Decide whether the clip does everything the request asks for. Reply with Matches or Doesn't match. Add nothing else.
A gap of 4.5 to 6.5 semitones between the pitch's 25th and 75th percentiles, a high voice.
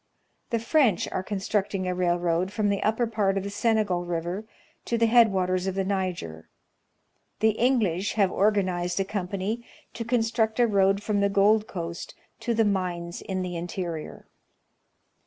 Doesn't match